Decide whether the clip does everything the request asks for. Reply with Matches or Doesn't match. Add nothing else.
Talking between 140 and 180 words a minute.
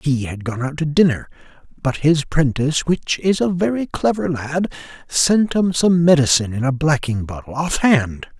Matches